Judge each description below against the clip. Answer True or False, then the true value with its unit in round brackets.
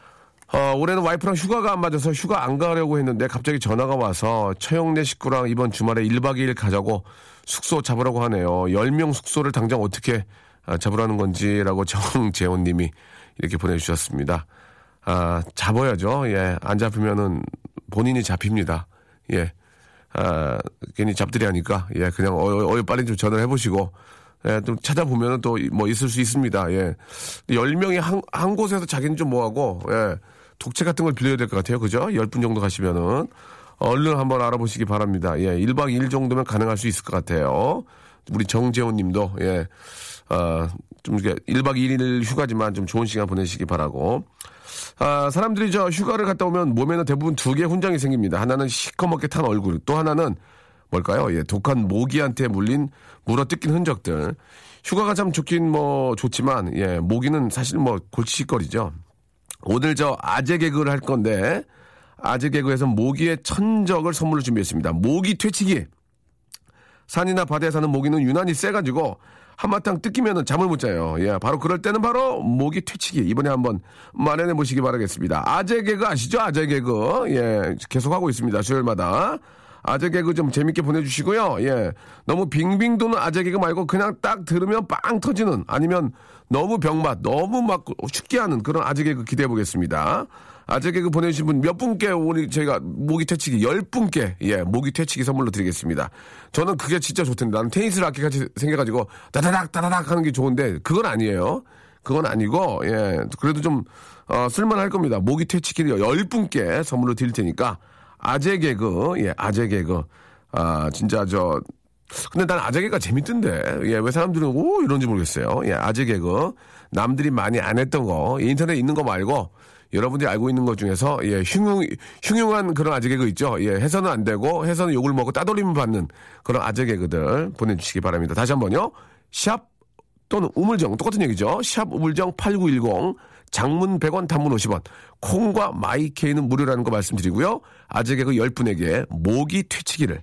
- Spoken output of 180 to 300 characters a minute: False (350 characters per minute)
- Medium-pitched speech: False (130 Hz)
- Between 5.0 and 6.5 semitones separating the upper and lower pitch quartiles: False (7.2 semitones)